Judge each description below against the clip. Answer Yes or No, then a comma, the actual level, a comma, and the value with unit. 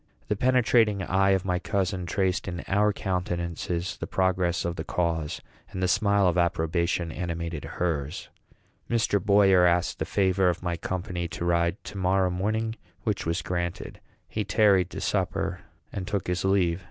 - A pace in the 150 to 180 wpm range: Yes, average, 165 wpm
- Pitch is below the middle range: Yes, very low, 90 Hz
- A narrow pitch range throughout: Yes, narrow, 2.2 semitones